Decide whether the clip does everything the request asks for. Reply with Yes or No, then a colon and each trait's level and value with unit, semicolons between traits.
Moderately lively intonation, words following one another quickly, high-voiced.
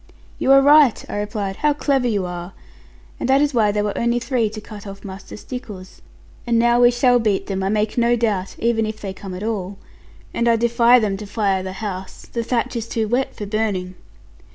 Yes: average, 3.3 semitones; fast, 220 wpm; high, 220 Hz